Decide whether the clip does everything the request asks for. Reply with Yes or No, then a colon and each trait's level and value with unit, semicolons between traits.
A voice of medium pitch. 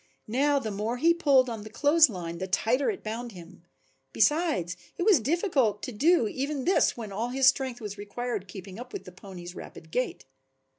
No: high, 235 Hz